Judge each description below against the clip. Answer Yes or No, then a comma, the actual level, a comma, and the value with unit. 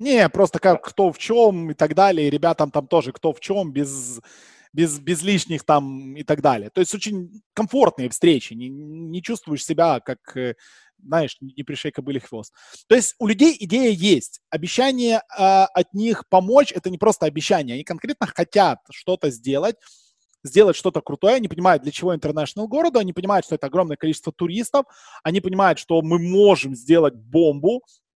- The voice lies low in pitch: No, medium, 175 Hz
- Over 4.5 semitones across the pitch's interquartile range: Yes, average, 5.3 semitones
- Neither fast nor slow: No, fast, 170 wpm